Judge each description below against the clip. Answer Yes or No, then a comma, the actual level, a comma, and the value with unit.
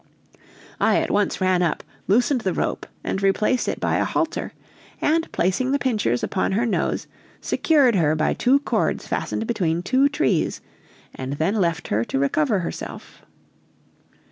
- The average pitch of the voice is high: Yes, high, 195 Hz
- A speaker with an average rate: Yes, average, 155 wpm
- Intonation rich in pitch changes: Yes, wide, 6.9 semitones